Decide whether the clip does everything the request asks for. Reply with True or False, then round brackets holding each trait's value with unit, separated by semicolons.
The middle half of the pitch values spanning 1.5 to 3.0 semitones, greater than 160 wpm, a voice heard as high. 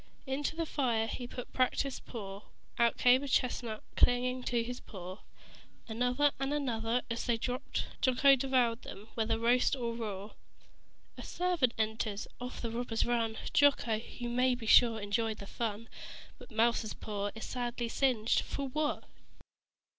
False (2.4 semitones; 155 wpm; 240 Hz)